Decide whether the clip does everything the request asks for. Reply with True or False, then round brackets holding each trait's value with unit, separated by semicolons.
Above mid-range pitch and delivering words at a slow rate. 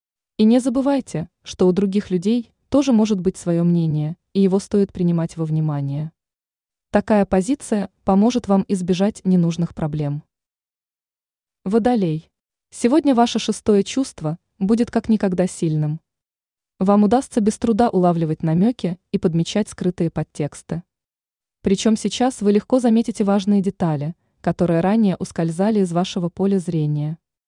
False (195 Hz; 125 wpm)